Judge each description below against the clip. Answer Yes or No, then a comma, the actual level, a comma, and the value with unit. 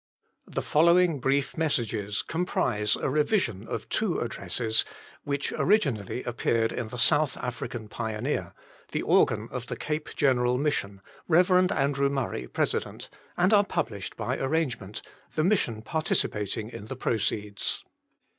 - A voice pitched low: Yes, low, 130 Hz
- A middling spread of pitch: No, wide, 5.9 semitones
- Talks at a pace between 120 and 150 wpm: Yes, average, 140 wpm